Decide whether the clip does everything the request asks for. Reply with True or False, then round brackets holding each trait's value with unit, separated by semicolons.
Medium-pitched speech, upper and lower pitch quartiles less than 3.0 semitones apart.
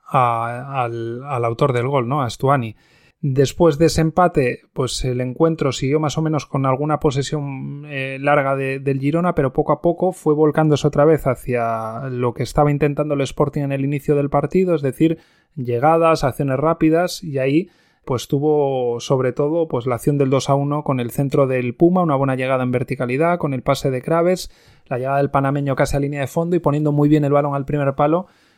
True (145 Hz; 2.6 semitones)